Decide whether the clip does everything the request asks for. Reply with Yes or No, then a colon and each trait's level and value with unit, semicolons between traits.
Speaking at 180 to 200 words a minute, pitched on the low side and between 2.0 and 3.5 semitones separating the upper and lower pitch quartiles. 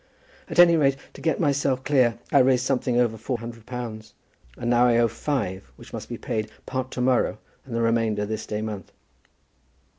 Yes: average, 190 wpm; low, 120 Hz; average, 2.9 semitones